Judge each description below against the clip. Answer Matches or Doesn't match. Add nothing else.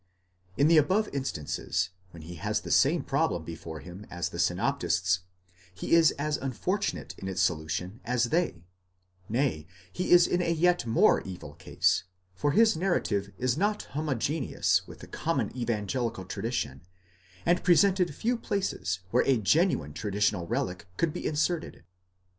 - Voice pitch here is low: Matches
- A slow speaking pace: Doesn't match